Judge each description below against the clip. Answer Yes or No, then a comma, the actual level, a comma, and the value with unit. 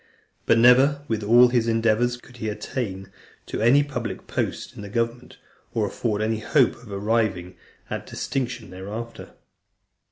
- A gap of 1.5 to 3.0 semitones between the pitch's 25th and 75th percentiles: Yes, narrow, 2.5 semitones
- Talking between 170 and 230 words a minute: No, average, 150 wpm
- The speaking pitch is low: Yes, low, 115 Hz